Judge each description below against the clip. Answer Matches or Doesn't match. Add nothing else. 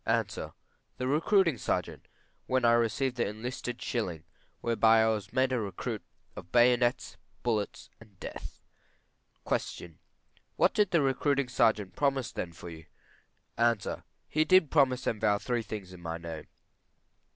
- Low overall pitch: Matches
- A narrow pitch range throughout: Doesn't match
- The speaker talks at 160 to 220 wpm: Doesn't match